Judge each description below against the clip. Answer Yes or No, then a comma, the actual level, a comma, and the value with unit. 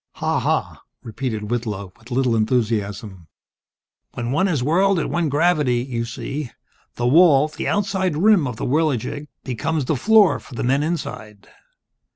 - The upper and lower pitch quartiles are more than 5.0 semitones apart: Yes, wide, 5.6 semitones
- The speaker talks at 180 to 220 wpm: No, average, 155 wpm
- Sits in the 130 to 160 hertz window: Yes, low, 135 Hz